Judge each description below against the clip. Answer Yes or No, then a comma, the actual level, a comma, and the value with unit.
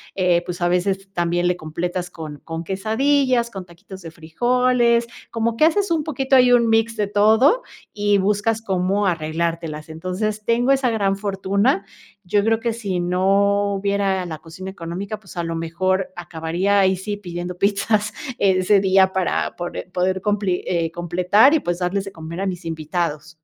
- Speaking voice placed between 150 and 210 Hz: Yes, high, 190 Hz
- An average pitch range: Yes, average, 3.5 semitones